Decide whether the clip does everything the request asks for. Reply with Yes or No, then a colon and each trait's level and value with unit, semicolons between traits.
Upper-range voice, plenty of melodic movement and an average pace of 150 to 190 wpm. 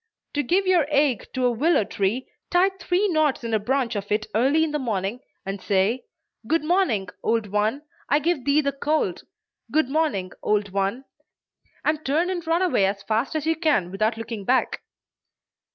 Yes: very high, 260 Hz; wide, 6.9 semitones; average, 185 wpm